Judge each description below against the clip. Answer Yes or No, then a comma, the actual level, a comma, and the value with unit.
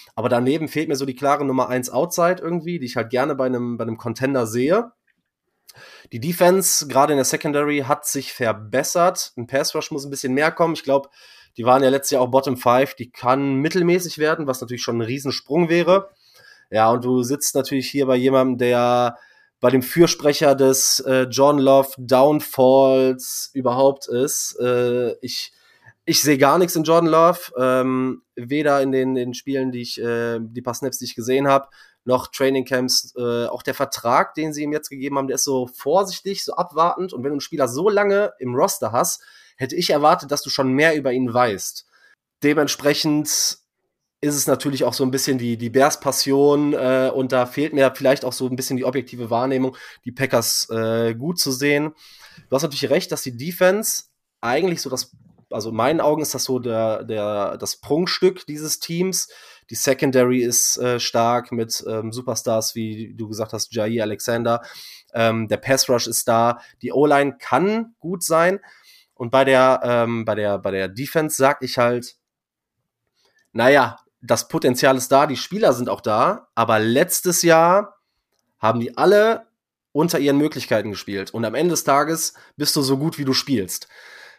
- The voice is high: No, low, 135 Hz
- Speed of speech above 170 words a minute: Yes, average, 185 wpm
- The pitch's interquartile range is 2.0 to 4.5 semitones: Yes, average, 3.4 semitones